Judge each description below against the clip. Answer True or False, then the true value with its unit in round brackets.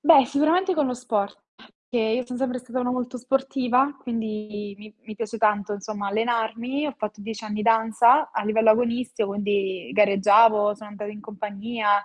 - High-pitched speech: True (225 Hz)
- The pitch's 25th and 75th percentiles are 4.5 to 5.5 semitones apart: False (3.1 semitones)